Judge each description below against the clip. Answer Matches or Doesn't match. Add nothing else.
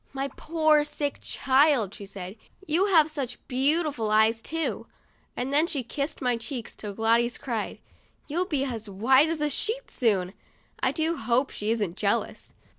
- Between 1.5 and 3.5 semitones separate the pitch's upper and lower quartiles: Doesn't match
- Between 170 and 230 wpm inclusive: Matches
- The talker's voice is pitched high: Matches